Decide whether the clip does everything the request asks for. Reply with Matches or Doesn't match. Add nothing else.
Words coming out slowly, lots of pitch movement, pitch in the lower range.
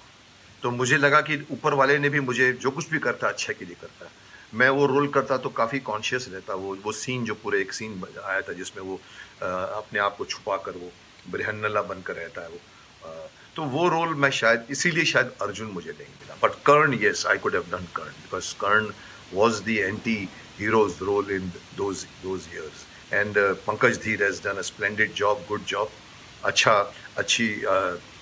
Doesn't match